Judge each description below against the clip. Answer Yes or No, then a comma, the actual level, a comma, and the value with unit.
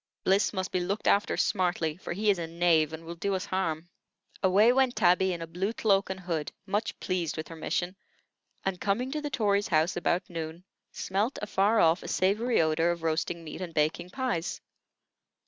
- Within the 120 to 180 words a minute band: No, average, 195 wpm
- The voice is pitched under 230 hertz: Yes, medium, 185 Hz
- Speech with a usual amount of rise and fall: Yes, average, 3.4 semitones